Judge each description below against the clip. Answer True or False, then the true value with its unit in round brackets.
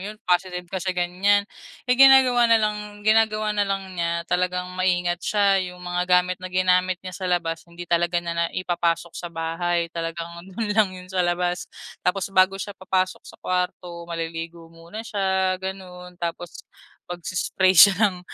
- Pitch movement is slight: True (1.9 semitones)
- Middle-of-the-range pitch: True (180 Hz)